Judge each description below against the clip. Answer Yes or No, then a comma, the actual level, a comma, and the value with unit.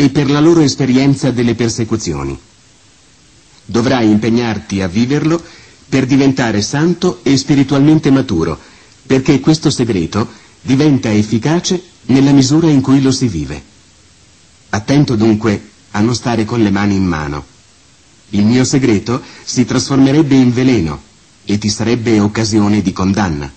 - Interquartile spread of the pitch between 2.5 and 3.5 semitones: No, average, 4.8 semitones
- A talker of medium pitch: No, low, 120 Hz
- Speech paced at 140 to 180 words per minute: No, average, 130 wpm